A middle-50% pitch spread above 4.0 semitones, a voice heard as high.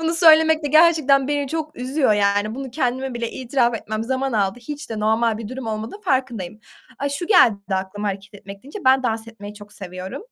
Yes: average, 5.1 semitones; high, 240 Hz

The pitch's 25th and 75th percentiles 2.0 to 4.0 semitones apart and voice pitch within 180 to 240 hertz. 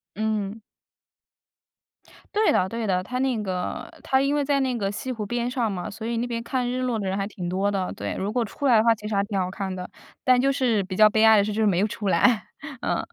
Yes: average, 3.7 semitones; high, 220 Hz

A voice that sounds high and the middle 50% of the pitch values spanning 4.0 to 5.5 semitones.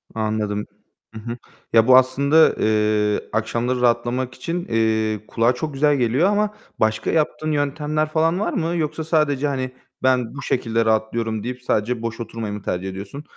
No: low, 125 Hz; average, 5.1 semitones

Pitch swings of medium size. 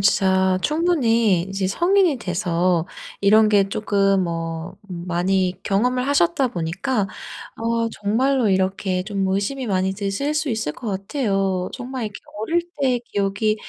Yes: average, 4.8 semitones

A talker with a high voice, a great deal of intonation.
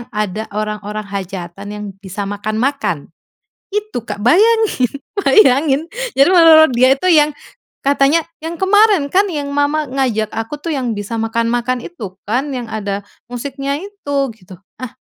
Yes: very high, 255 Hz; wide, 6.3 semitones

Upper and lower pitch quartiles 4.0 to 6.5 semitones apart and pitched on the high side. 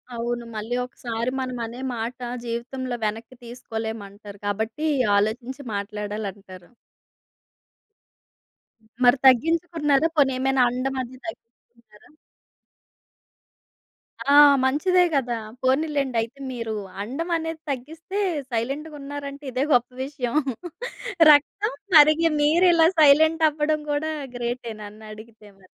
Yes: average, 4.7 semitones; very high, 255 Hz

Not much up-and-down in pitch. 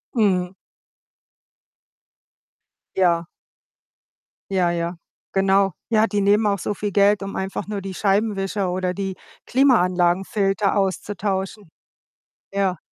Yes: narrow, 1.8 semitones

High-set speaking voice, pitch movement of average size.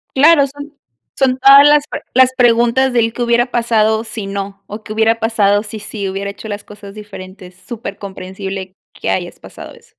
Yes: high, 220 Hz; average, 3.5 semitones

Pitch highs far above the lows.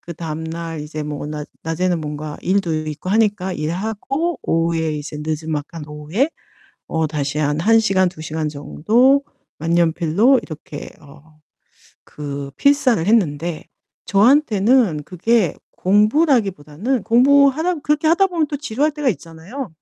Yes: wide, 7.5 semitones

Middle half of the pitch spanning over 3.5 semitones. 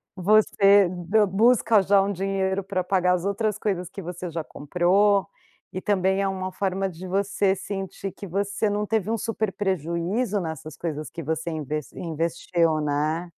No: average, 2.8 semitones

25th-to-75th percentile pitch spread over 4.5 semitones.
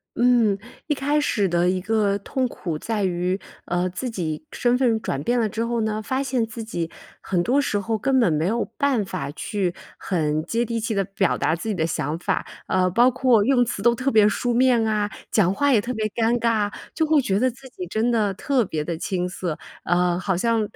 Yes: average, 4.9 semitones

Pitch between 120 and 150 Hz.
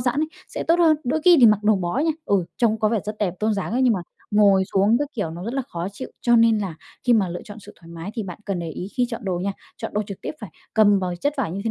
No: high, 210 Hz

